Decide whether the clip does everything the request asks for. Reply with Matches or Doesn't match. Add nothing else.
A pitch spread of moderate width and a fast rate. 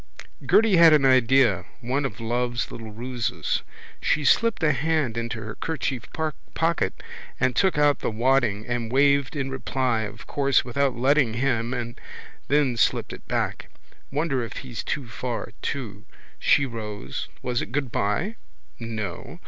Doesn't match